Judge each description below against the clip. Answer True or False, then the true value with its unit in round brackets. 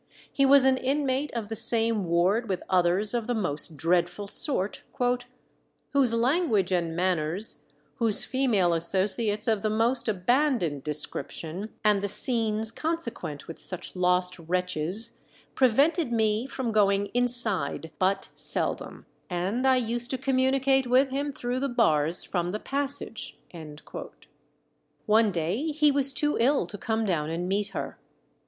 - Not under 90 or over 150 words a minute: True (140 wpm)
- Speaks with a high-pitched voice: True (220 Hz)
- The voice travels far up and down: True (6.1 semitones)